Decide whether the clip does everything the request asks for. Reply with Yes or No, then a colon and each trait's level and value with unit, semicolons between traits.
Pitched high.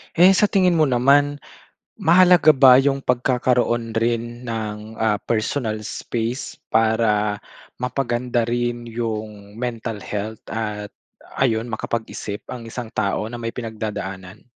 No: low, 115 Hz